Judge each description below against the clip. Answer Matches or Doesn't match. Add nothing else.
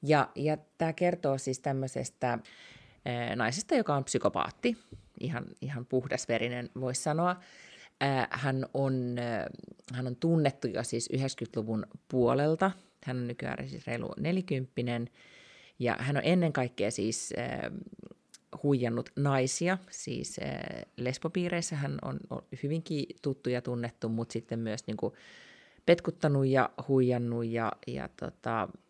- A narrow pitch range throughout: Doesn't match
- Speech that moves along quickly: Doesn't match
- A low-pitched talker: Matches